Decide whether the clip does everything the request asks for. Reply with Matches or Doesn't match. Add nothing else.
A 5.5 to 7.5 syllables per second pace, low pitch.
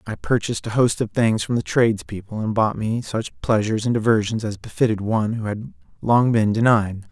Matches